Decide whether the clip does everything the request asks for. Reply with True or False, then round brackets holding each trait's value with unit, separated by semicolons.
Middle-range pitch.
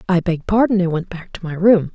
True (180 Hz)